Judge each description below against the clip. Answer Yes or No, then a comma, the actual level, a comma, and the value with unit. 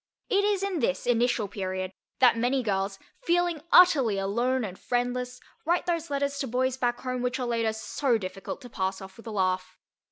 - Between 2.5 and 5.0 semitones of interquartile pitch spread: No, wide, 5.5 semitones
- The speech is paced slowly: No, average, 190 wpm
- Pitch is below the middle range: No, high, 245 Hz